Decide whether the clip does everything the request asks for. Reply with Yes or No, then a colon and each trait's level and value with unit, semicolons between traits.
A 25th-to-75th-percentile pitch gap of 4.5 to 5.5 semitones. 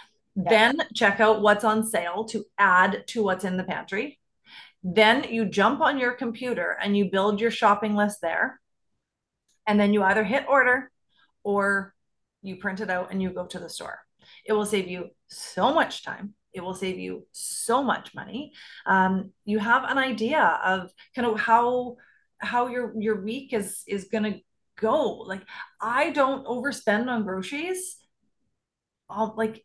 No: average, 3.8 semitones